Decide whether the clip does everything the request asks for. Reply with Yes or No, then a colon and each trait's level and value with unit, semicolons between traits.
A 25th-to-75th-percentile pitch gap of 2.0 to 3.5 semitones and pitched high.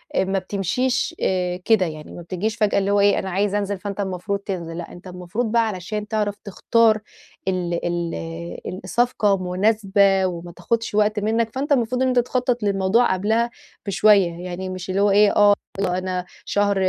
Yes: average, 3.0 semitones; high, 200 Hz